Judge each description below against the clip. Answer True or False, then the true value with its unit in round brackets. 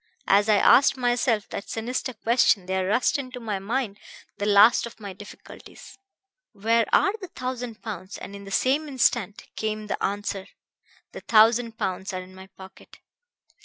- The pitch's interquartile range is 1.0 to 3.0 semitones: False (3.5 semitones)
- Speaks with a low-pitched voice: False (215 Hz)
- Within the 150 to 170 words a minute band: True (165 wpm)